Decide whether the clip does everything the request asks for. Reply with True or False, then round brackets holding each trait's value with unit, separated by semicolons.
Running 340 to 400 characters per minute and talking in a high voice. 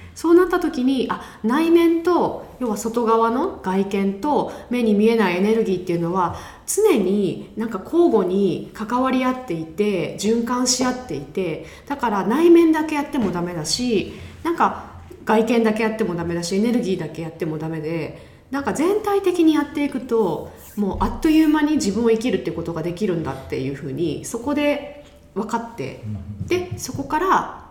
True (355 characters per minute; 225 Hz)